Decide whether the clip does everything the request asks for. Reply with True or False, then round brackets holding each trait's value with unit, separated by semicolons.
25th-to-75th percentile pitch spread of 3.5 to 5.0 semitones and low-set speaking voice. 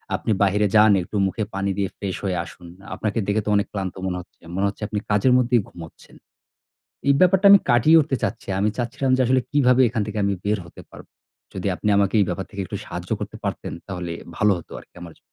True (3.9 semitones; 105 Hz)